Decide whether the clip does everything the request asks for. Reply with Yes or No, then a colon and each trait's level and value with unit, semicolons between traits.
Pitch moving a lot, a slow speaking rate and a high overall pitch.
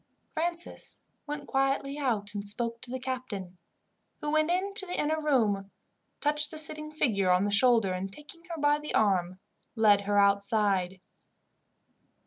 No: wide, 6.9 semitones; average, 155 wpm; very high, 250 Hz